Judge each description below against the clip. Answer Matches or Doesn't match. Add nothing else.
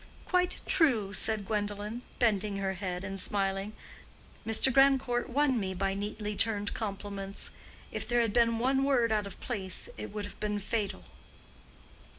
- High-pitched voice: Matches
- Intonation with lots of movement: Doesn't match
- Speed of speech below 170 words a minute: Matches